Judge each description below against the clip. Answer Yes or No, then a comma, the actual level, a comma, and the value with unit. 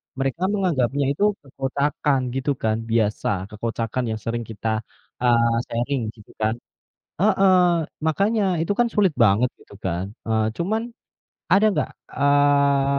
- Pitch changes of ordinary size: No, wide, 7.3 semitones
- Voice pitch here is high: No, low, 135 Hz